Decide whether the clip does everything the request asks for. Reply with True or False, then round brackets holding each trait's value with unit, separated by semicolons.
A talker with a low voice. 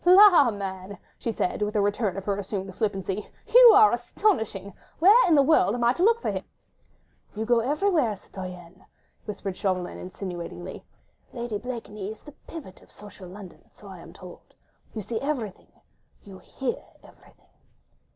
False (210 Hz)